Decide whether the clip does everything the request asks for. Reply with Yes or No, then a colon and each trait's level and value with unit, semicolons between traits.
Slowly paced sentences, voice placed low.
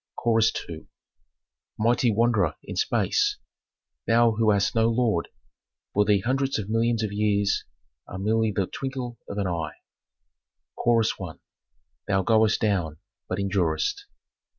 Yes: slow, 130 wpm; low, 110 Hz